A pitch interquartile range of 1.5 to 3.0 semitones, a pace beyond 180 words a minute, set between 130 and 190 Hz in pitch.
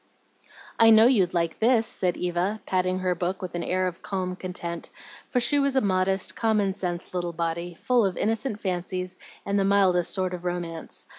Yes: narrow, 2.5 semitones; average, 190 wpm; medium, 185 Hz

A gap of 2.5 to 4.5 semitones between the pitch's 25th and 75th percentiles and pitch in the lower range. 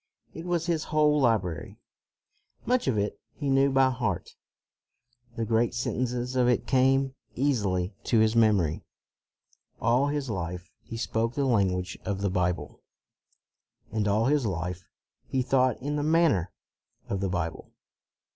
No: wide, 5.5 semitones; low, 120 Hz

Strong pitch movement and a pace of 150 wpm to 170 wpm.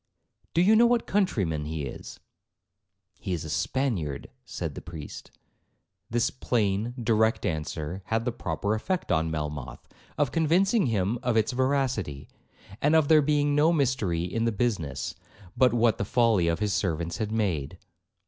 Yes: wide, 8.2 semitones; average, 160 wpm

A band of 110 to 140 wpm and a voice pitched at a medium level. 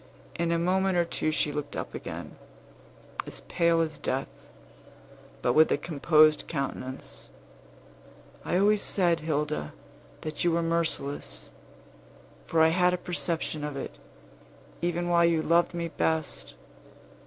Yes: slow, 135 wpm; medium, 165 Hz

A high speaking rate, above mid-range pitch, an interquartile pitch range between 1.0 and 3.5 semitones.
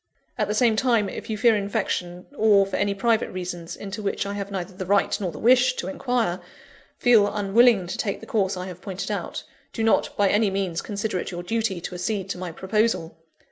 Yes: fast, 220 wpm; high, 200 Hz; average, 3.1 semitones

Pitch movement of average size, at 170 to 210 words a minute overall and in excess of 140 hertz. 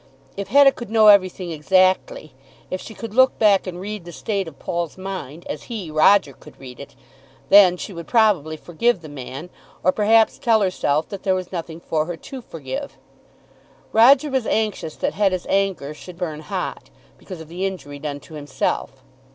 Yes: average, 4.9 semitones; average, 185 wpm; medium, 185 Hz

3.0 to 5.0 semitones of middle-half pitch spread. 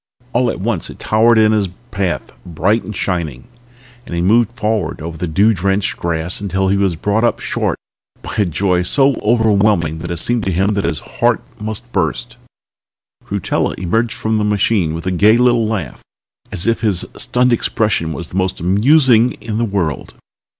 Yes: average, 4.3 semitones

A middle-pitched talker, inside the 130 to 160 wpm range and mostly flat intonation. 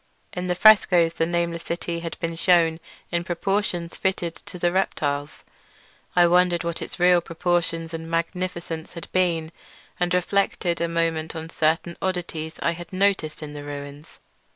Yes: medium, 170 Hz; average, 155 wpm; narrow, 1.6 semitones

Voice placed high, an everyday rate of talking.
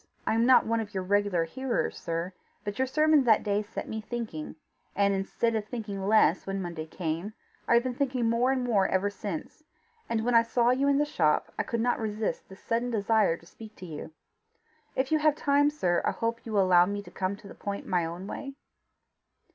No: high, 215 Hz; fast, 220 wpm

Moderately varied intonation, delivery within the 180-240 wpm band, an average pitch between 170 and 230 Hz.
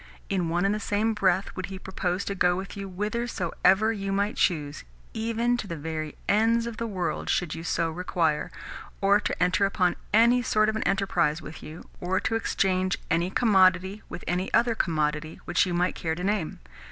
Yes: average, 3.3 semitones; average, 195 wpm; high, 190 Hz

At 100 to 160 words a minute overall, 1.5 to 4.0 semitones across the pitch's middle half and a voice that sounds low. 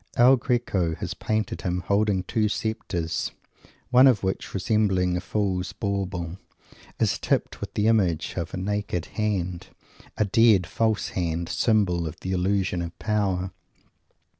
Yes: average, 140 wpm; average, 3.2 semitones; very low, 95 Hz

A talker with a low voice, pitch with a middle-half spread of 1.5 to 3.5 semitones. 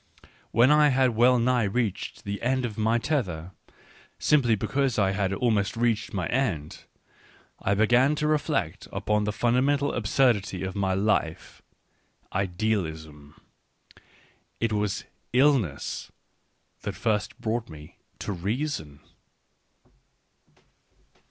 No: low, 110 Hz; average, 4.6 semitones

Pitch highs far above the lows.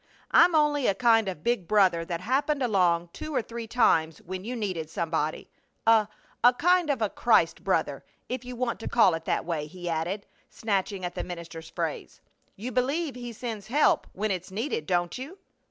Yes: wide, 6.1 semitones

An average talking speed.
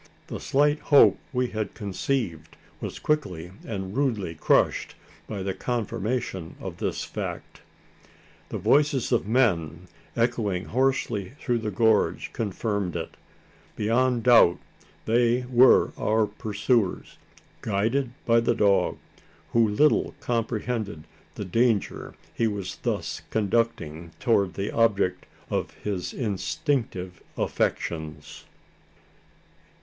No: slow, 110 wpm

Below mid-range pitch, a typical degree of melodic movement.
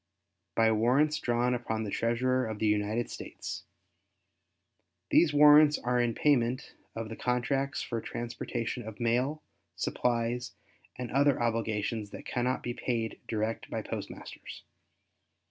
No: low, 120 Hz; narrow, 2.2 semitones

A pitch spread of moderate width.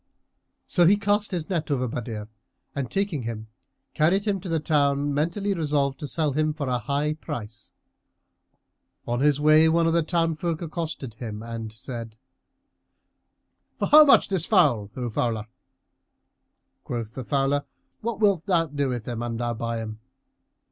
No: wide, 5.8 semitones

